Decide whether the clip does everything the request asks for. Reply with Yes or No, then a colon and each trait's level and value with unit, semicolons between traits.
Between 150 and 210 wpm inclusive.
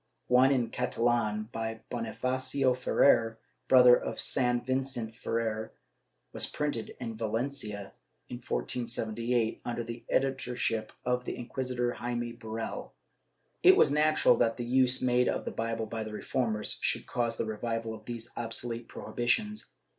No: average, 140 wpm